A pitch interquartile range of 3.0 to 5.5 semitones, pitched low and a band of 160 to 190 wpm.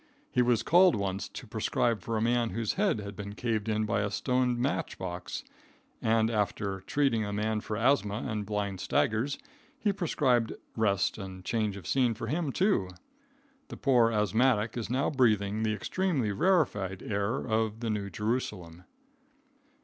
Yes: average, 3.4 semitones; low, 110 Hz; average, 165 wpm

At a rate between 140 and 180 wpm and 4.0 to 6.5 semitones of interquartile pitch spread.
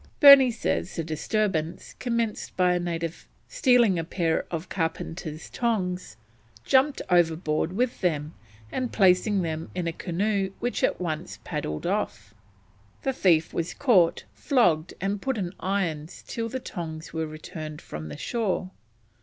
Yes: average, 145 wpm; average, 5.0 semitones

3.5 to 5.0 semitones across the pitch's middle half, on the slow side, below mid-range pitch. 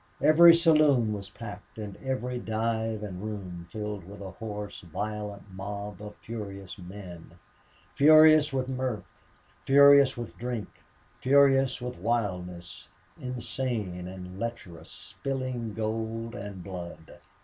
Yes: average, 4.5 semitones; slow, 115 wpm; low, 110 Hz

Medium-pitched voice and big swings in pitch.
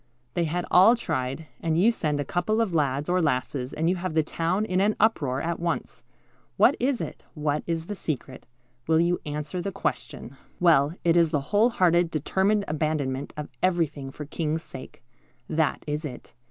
No: medium, 165 Hz; average, 3.5 semitones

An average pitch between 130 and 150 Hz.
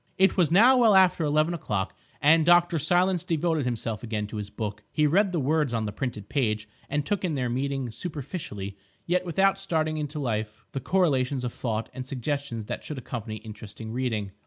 Yes: medium, 140 Hz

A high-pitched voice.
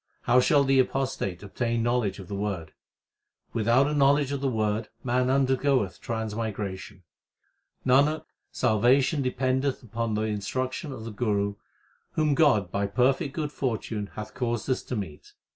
No: low, 120 Hz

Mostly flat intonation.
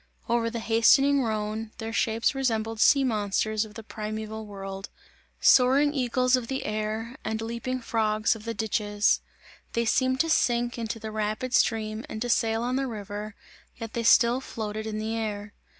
Yes: narrow, 1.9 semitones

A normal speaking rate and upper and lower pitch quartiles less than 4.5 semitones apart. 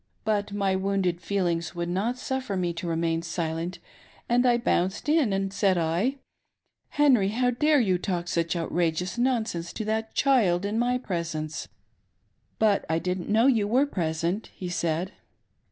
No: average, 170 wpm; average, 5.0 semitones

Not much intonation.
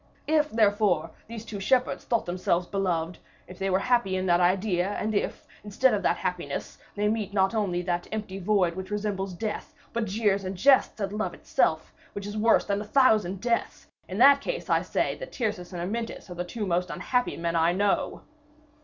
No: average, 3.4 semitones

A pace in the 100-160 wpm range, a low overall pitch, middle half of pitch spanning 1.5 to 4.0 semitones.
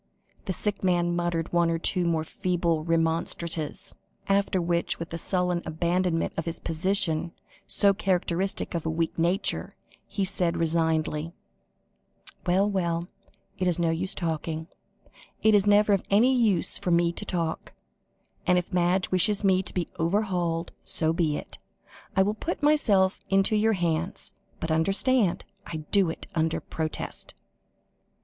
No: average, 150 wpm; medium, 175 Hz; average, 2.8 semitones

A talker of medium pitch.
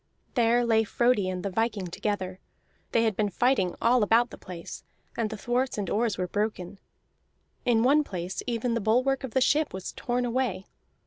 No: high, 225 Hz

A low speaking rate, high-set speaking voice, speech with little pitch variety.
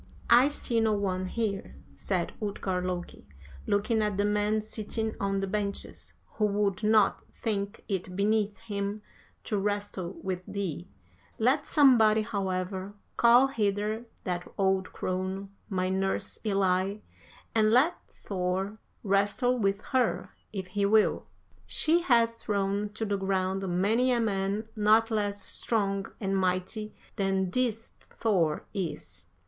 Yes: slow, 130 wpm; high, 205 Hz; narrow, 2.2 semitones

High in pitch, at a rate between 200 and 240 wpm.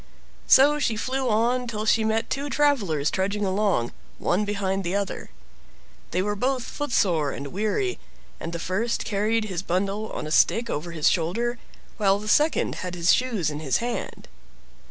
No: high, 205 Hz; average, 175 wpm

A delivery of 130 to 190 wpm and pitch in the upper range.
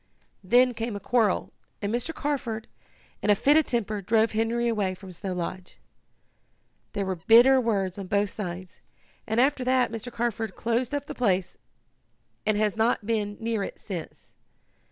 Yes: average, 165 wpm; high, 220 Hz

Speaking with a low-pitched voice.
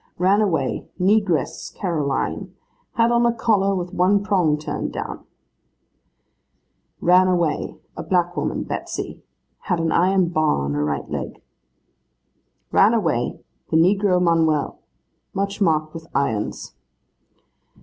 No: medium, 180 Hz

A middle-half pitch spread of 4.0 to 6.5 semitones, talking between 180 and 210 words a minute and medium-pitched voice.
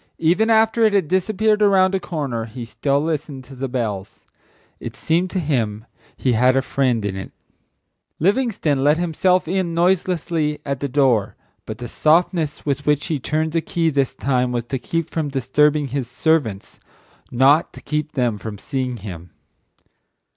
No: average, 5.1 semitones; average, 170 wpm; medium, 145 Hz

